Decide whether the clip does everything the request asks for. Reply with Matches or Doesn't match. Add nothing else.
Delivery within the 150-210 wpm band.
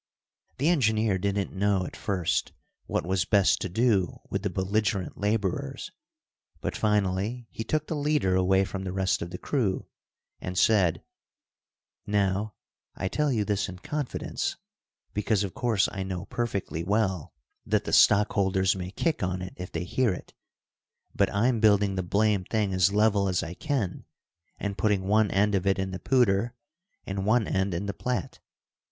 Matches